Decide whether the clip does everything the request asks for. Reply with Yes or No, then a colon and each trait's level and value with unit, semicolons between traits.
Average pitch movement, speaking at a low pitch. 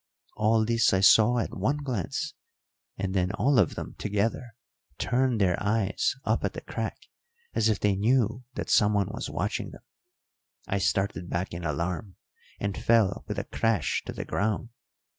Yes: average, 3.2 semitones; low, 105 Hz